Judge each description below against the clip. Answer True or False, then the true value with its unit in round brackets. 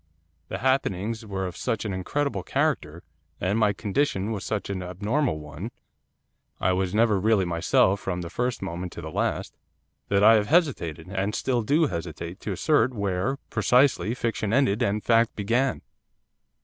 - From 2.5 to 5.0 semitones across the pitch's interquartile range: True (4.7 semitones)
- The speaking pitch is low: True (105 Hz)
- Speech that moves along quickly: False (160 wpm)